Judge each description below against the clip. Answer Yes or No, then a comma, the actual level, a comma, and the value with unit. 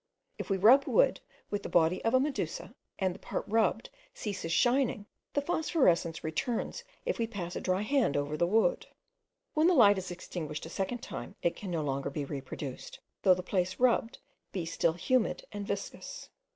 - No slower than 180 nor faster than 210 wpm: Yes, average, 185 wpm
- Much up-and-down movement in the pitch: Yes, wide, 6.1 semitones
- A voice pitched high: Yes, high, 195 Hz